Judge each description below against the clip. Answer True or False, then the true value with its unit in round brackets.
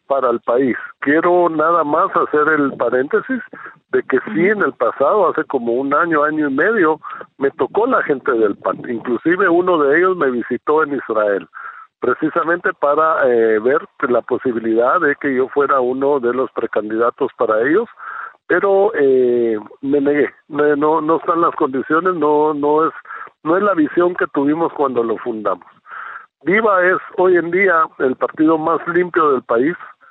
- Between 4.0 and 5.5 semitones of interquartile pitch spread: True (4.3 semitones)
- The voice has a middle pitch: True (155 Hz)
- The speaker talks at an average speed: True (165 wpm)